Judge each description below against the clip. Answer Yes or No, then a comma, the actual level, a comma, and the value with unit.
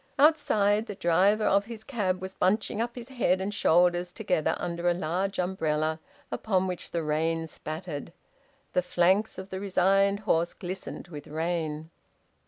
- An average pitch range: Yes, average, 3.4 semitones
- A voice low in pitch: No, medium, 185 Hz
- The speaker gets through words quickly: No, average, 155 wpm